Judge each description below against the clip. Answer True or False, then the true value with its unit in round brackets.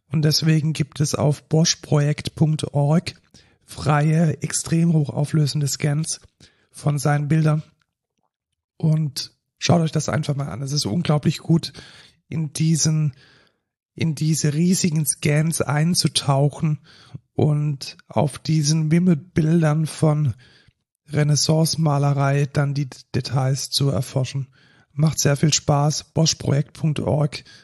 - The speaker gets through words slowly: True (100 wpm)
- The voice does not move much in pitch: True (2.0 semitones)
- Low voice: False (150 Hz)